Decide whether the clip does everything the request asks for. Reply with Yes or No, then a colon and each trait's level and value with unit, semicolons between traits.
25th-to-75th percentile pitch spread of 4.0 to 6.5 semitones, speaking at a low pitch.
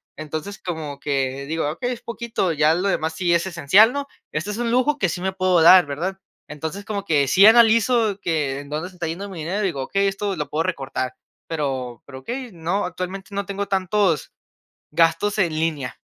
No: average, 4.6 semitones; medium, 180 Hz